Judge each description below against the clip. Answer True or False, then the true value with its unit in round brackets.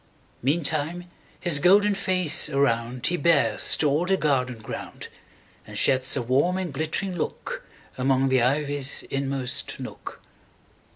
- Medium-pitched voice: True (145 Hz)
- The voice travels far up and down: False (4.9 semitones)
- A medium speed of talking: False (115 wpm)